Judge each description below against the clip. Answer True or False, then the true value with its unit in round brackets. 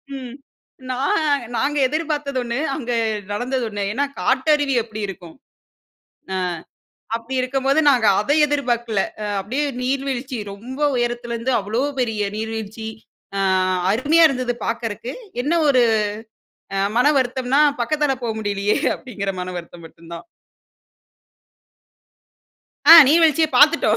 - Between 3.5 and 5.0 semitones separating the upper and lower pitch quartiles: True (4.2 semitones)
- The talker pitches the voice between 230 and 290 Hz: True (250 Hz)